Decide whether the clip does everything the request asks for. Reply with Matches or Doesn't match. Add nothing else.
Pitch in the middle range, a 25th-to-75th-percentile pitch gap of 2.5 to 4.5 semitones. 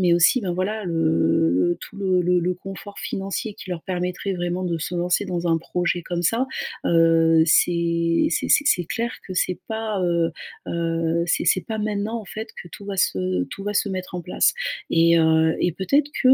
Matches